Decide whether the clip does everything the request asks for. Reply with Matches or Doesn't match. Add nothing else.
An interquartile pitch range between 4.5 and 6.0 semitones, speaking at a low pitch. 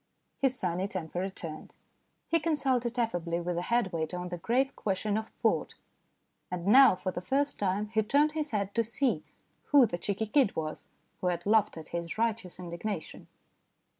Doesn't match